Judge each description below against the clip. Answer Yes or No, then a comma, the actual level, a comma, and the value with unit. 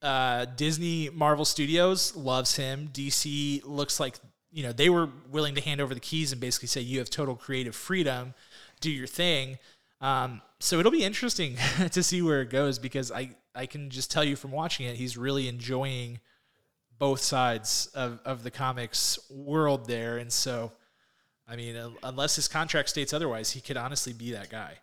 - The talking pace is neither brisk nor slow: Yes, average, 185 wpm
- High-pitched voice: No, low, 135 Hz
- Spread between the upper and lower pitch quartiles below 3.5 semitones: Yes, average, 3.1 semitones